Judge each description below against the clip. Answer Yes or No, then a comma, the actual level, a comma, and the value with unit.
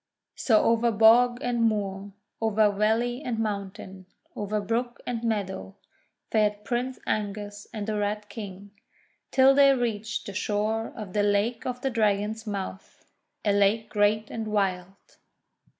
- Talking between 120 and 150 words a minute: Yes, average, 145 wpm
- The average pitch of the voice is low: No, high, 215 Hz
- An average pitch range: No, narrow, 2.1 semitones